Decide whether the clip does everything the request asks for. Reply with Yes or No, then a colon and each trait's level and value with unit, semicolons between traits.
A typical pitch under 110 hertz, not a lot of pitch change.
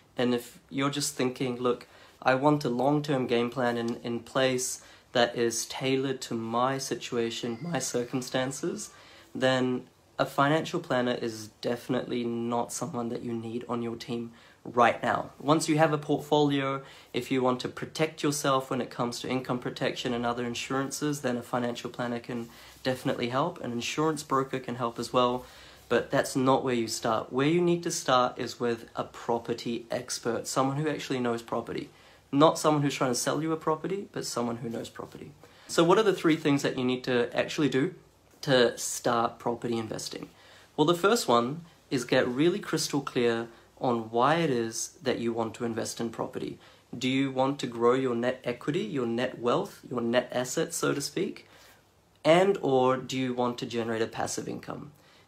No: low, 125 Hz; narrow, 2.3 semitones